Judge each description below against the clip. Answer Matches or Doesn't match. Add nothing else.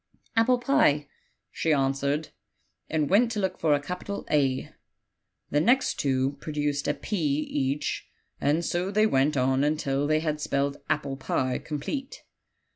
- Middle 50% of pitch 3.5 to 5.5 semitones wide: Matches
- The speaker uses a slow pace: Doesn't match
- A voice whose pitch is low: Doesn't match